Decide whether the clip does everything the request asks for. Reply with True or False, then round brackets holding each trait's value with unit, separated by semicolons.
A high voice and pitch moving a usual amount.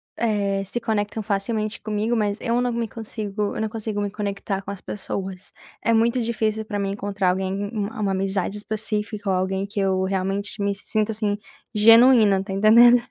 False (205 Hz; 2.0 semitones)